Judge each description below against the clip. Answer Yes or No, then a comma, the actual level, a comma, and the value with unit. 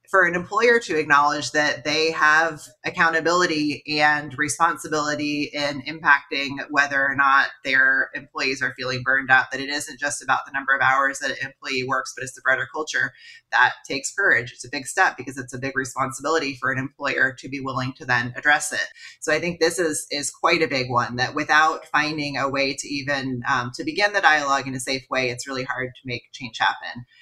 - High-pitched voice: No, medium, 140 Hz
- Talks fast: Yes, fast, 210 wpm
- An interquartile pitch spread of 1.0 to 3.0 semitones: Yes, narrow, 2.5 semitones